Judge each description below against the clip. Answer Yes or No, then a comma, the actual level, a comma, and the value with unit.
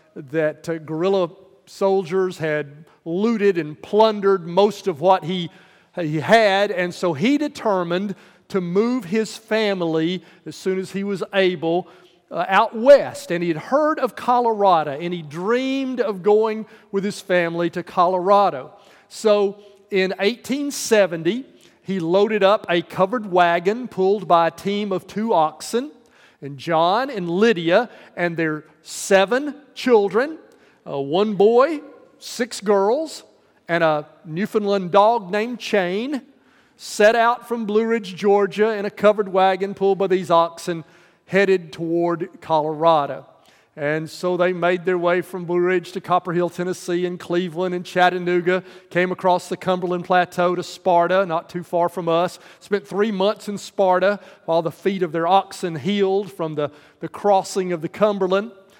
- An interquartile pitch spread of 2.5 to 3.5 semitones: Yes, average, 3.0 semitones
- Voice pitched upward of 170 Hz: Yes, high, 190 Hz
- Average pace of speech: Yes, average, 150 wpm